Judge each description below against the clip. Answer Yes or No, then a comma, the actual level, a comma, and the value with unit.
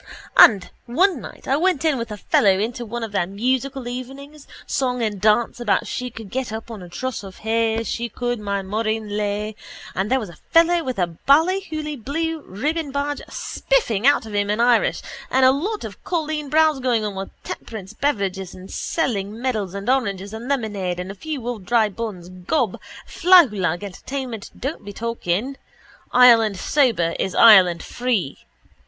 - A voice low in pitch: No, high, 230 Hz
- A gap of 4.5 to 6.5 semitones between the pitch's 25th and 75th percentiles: Yes, average, 5.1 semitones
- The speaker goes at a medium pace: Yes, average, 175 wpm